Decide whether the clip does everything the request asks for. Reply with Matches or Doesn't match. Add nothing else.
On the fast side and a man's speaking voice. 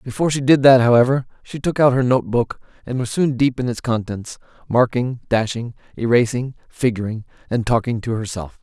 Doesn't match